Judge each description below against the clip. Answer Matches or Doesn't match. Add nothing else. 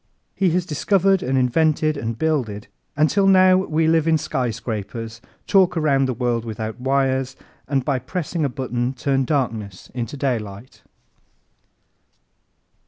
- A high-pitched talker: Doesn't match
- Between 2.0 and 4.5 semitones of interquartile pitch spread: Doesn't match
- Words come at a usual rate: Doesn't match